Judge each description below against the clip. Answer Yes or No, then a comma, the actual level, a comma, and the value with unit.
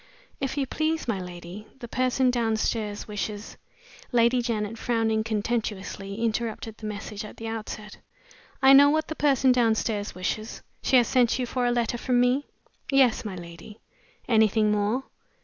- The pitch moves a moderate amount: Yes, average, 3.0 semitones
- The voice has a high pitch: Yes, high, 225 Hz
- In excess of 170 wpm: No, average, 160 wpm